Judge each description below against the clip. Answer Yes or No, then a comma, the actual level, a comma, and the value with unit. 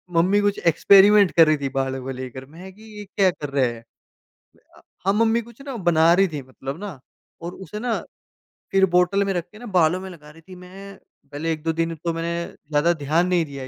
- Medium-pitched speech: Yes, medium, 170 Hz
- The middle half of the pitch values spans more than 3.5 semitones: Yes, average, 4.5 semitones